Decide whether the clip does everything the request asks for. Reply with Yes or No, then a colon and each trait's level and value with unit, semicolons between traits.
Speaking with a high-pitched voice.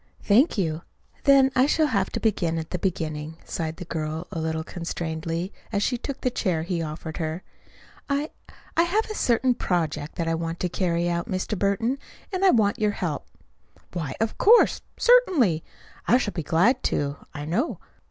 No: medium, 180 Hz